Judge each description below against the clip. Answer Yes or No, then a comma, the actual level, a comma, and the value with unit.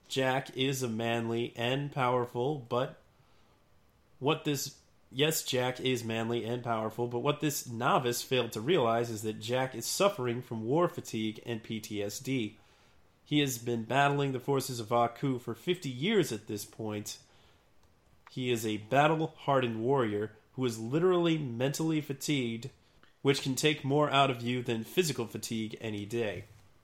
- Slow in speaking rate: No, average, 155 wpm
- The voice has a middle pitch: No, low, 120 Hz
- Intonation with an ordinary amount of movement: Yes, average, 3.5 semitones